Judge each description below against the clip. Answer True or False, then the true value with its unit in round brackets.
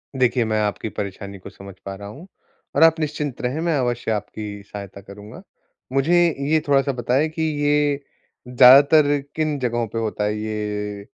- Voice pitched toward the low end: True (120 Hz)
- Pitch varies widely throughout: True (5.9 semitones)